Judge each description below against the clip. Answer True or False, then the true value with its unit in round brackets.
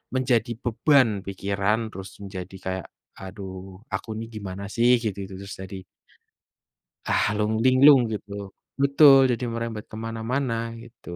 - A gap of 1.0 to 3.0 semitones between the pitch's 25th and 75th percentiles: False (3.9 semitones)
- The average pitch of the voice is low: True (110 Hz)